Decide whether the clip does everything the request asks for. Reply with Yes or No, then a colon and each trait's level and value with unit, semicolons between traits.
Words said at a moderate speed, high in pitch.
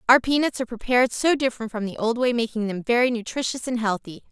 No: fast, 225 wpm; high, 235 Hz